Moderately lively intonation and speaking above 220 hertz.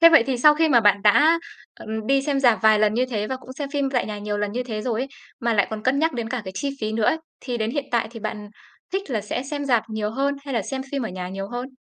Yes: average, 4.3 semitones; high, 240 Hz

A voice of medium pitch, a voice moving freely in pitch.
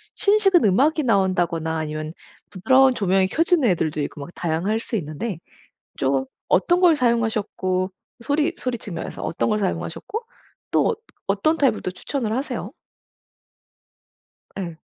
No: high, 210 Hz; wide, 7.4 semitones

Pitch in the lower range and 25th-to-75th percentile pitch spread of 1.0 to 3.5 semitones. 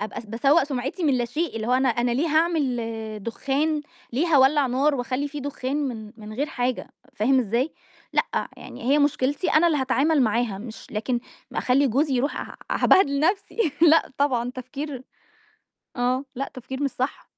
No: very high, 265 Hz; average, 3.2 semitones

